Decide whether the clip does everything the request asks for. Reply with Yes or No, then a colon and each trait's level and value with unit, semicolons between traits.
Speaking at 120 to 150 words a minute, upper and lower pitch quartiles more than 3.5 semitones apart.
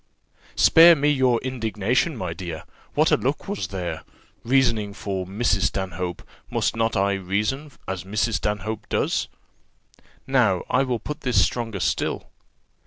Yes: average, 140 wpm; average, 5.0 semitones